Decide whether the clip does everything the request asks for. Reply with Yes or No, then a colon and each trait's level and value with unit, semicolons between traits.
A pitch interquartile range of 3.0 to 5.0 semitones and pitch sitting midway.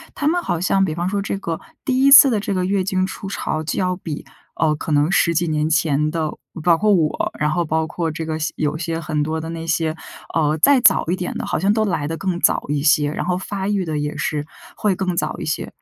Yes: average, 3.5 semitones; medium, 165 Hz